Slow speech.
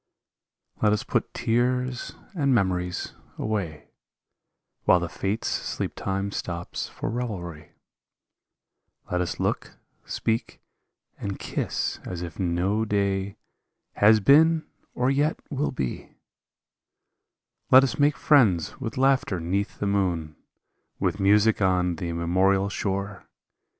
Yes: slow, 115 wpm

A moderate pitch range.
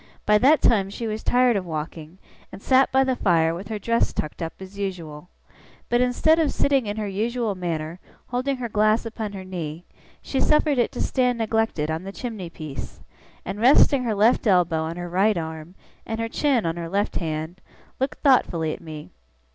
No: wide, 6.1 semitones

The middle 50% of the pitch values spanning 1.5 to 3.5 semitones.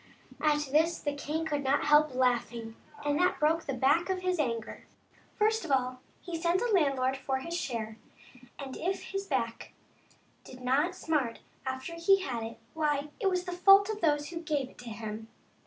No: average, 4.9 semitones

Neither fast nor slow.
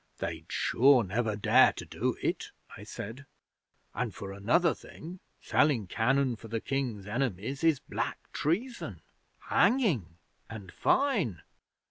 No: slow, 125 wpm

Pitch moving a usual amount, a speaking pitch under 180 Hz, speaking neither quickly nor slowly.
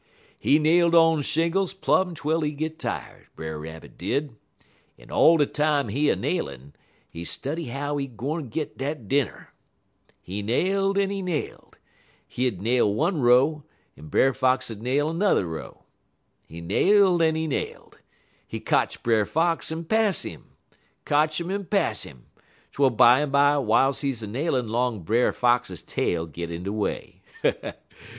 No: wide, 6.3 semitones; medium, 140 Hz; average, 155 wpm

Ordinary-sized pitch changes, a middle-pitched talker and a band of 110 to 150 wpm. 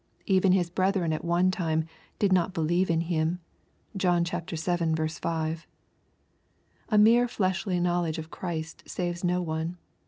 No: narrow, 2.3 semitones; medium, 175 Hz; average, 145 wpm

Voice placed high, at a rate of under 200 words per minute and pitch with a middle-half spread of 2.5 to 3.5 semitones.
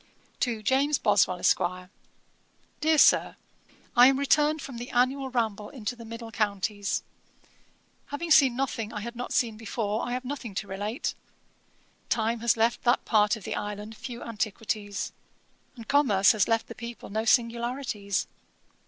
Yes: high, 230 Hz; average, 155 wpm; average, 3.2 semitones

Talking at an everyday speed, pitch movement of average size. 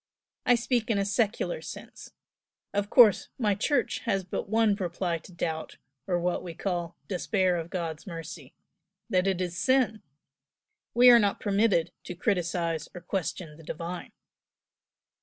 Yes: average, 155 wpm; average, 3.7 semitones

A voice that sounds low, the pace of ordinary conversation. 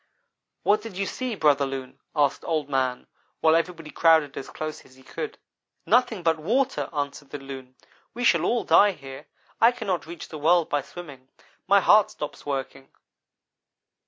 No: medium, 155 Hz; average, 165 wpm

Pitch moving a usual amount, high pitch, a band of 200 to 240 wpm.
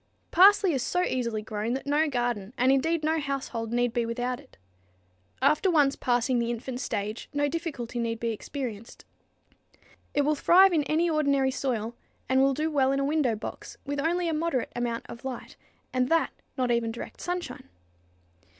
No: average, 4.3 semitones; very high, 265 Hz; average, 180 wpm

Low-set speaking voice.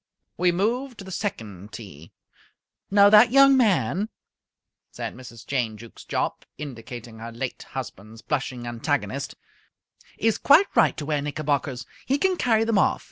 No: medium, 150 Hz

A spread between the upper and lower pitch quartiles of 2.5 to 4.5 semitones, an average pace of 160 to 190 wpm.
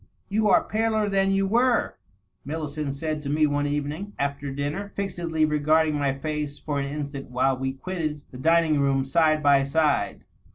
Yes: average, 3.0 semitones; average, 175 wpm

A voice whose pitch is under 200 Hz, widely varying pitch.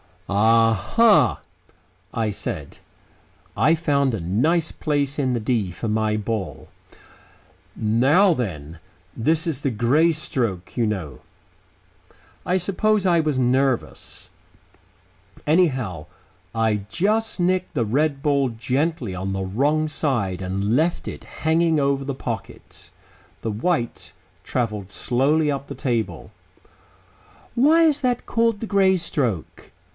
Yes: low, 135 Hz; wide, 6.8 semitones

